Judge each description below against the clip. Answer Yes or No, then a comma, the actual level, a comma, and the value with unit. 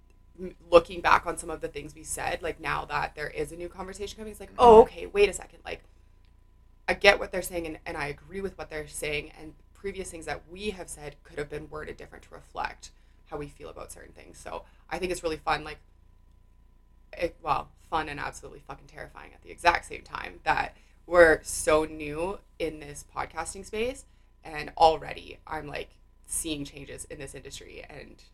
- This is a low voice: No, medium, 155 Hz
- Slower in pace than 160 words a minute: No, fast, 205 wpm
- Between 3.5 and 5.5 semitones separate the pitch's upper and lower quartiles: Yes, average, 4.1 semitones